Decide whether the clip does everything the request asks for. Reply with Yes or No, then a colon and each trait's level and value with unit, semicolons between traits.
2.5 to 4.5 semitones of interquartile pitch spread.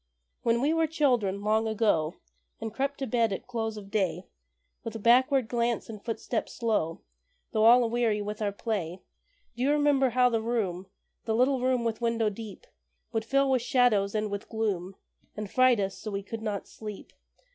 Yes: average, 3.1 semitones